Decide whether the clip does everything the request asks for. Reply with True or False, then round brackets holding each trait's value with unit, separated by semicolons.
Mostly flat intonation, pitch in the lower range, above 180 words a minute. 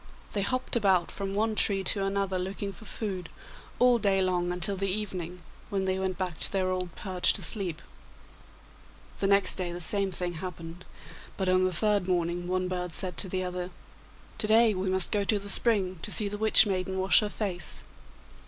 False (1.9 semitones; 190 Hz; 200 wpm)